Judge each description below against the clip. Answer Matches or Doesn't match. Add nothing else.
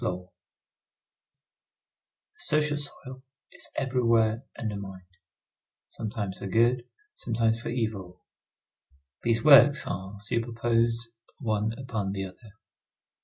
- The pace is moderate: Doesn't match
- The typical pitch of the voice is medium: Doesn't match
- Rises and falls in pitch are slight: Doesn't match